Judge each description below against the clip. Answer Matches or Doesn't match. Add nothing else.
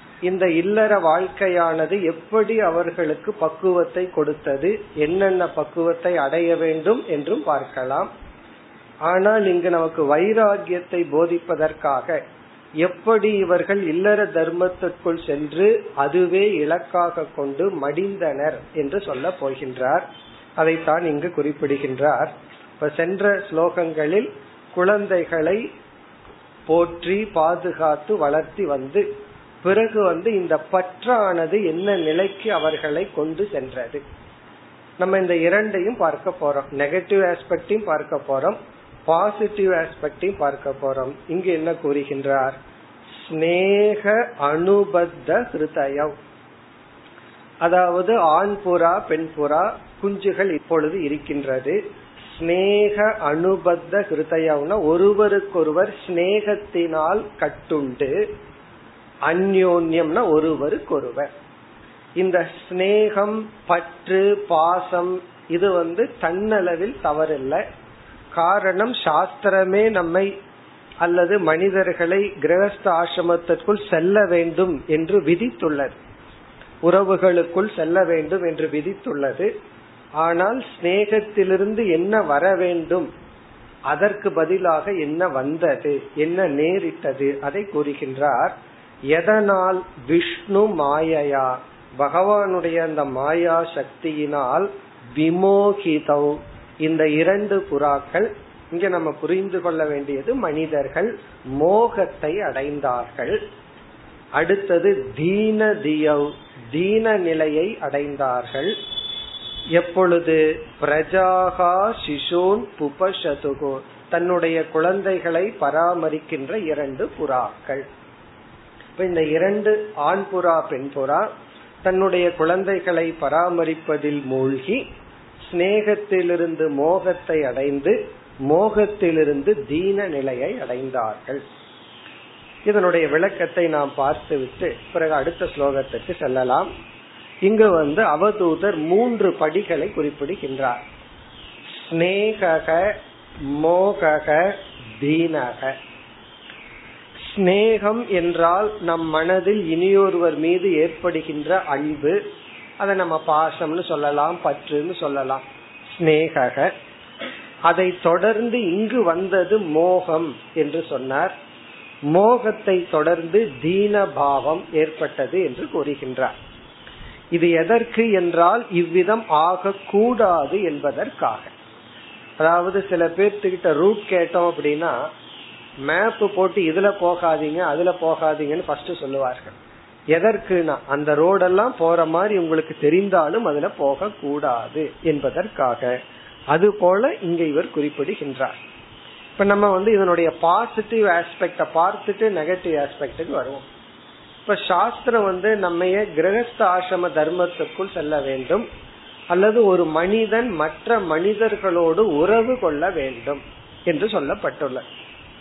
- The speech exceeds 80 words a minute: Doesn't match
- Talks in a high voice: Doesn't match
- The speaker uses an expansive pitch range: Doesn't match